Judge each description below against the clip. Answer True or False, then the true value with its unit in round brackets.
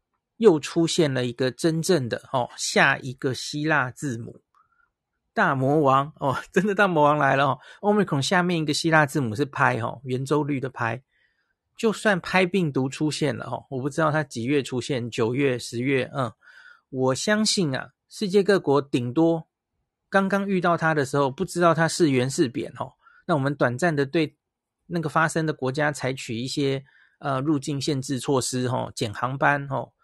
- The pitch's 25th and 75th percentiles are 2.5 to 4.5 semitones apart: True (4.2 semitones)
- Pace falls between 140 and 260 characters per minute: True (255 characters per minute)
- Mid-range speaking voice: True (145 Hz)